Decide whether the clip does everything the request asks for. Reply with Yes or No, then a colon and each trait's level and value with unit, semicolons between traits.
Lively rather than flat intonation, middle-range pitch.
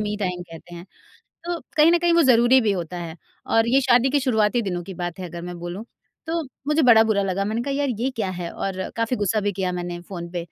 No: wide, 6.0 semitones; high, 205 Hz